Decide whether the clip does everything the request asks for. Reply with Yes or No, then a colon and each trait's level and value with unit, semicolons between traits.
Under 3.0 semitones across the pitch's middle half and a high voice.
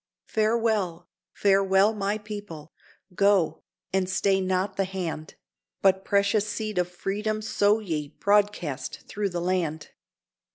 Yes: narrow, 2.6 semitones; high, 195 Hz